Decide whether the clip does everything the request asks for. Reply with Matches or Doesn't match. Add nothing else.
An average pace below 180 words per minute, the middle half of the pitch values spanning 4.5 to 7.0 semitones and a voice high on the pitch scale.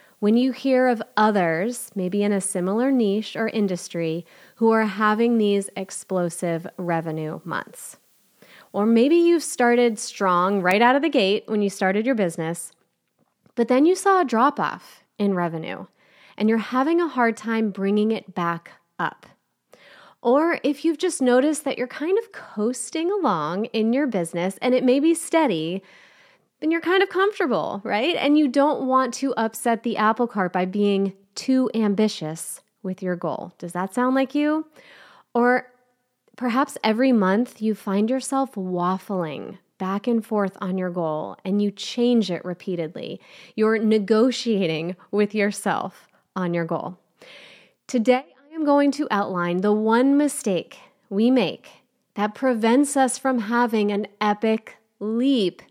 Matches